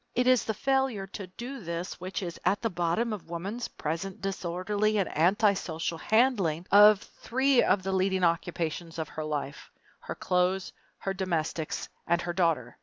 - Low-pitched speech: No, medium, 185 Hz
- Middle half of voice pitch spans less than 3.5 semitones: No, average, 3.9 semitones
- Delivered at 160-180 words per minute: Yes, average, 165 wpm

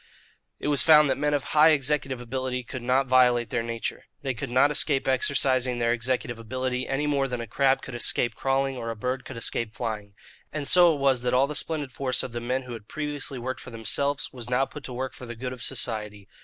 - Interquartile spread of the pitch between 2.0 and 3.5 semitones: Yes, narrow, 2.4 semitones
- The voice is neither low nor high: No, low, 130 Hz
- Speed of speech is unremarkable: No, fast, 235 wpm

